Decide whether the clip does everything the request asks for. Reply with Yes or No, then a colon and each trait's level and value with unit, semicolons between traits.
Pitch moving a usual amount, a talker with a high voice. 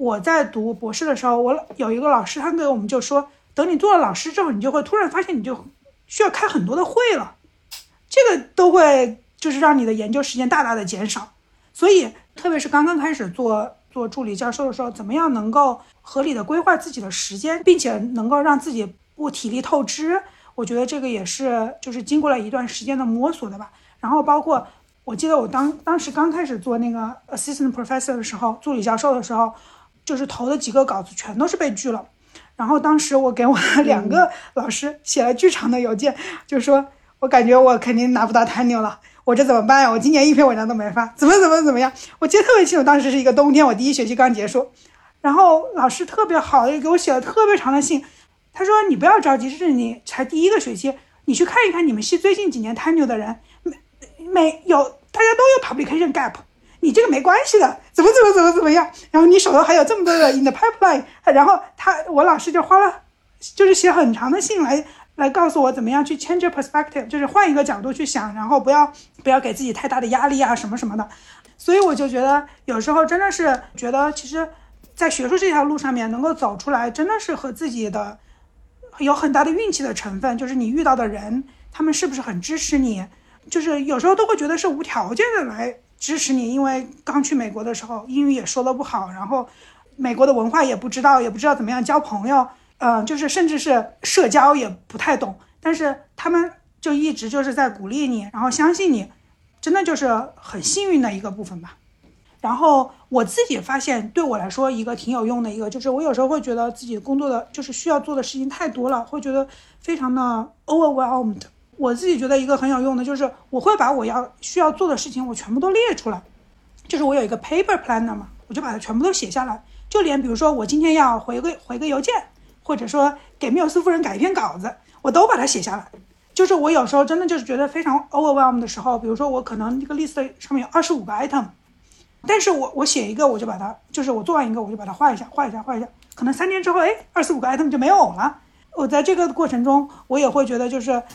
Yes: average, 4.6 semitones; very high, 275 Hz